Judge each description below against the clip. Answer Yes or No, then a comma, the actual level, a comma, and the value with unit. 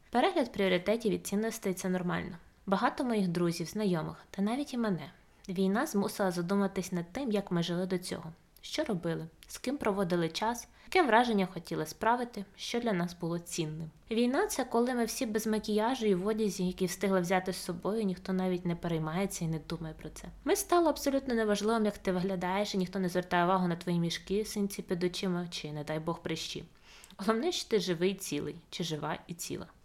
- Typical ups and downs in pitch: Yes, average, 3.8 semitones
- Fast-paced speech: Yes, fast, 190 wpm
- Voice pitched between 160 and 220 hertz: Yes, high, 190 Hz